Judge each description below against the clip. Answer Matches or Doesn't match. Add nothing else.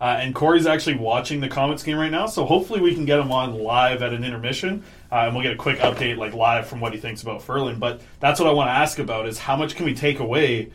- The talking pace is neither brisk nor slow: Doesn't match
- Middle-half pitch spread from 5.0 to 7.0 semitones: Doesn't match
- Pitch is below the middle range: Matches